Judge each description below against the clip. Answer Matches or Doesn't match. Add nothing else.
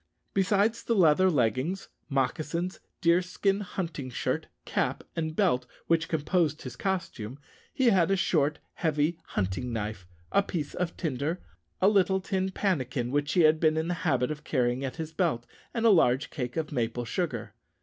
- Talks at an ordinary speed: Matches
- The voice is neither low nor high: Matches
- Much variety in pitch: Matches